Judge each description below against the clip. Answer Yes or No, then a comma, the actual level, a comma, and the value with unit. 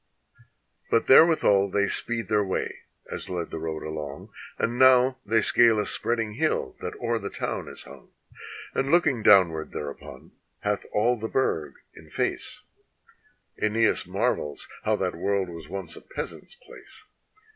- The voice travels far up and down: Yes, wide, 6.3 semitones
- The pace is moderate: Yes, average, 155 wpm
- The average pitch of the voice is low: Yes, low, 105 Hz